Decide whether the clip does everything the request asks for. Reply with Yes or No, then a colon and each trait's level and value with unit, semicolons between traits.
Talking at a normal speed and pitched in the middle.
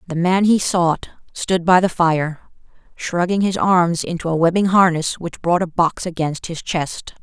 Yes: average, 185 wpm; medium, 175 Hz